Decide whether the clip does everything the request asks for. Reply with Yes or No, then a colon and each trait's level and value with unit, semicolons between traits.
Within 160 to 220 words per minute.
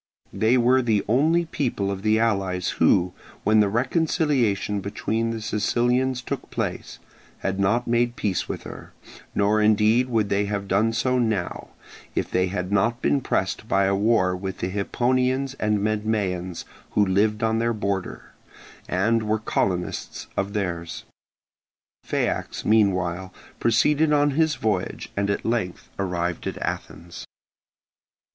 No: average, 140 wpm